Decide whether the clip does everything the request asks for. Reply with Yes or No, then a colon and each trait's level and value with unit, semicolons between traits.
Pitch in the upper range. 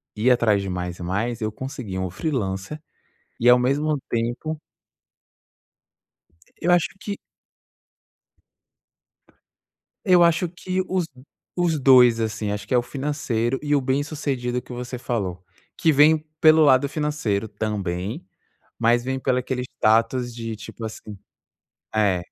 No: low, 125 Hz